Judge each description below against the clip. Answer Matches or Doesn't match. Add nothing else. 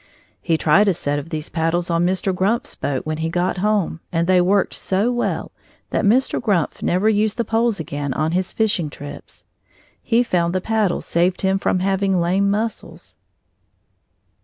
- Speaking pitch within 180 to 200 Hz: Matches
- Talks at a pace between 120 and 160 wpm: Doesn't match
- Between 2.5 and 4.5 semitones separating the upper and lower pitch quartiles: Matches